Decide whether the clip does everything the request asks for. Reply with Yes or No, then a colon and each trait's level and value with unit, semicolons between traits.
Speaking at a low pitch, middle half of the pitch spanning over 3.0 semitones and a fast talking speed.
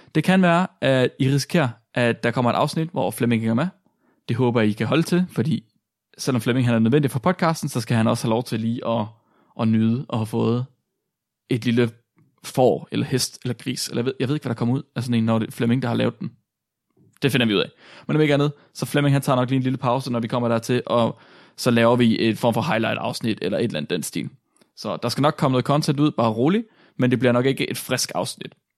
Yes: low, 125 Hz; average, 3.4 semitones; fast, 265 wpm